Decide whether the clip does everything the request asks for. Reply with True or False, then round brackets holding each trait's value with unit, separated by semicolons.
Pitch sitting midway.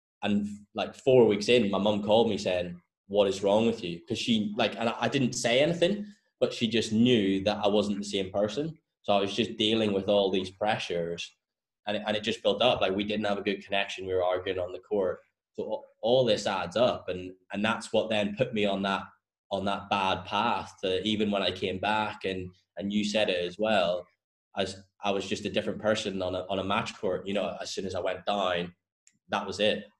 False (100 Hz)